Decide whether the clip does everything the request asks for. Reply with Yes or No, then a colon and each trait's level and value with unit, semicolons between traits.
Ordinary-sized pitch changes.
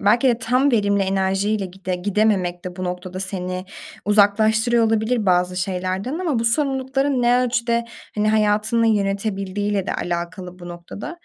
Yes: average, 3.9 semitones